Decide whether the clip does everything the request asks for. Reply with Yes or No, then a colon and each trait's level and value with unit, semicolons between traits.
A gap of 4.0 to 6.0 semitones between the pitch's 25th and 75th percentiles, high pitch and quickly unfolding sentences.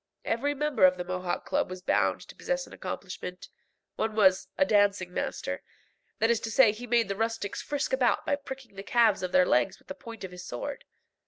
Yes: wide, 5.4 semitones; high, 220 Hz; fast, 215 wpm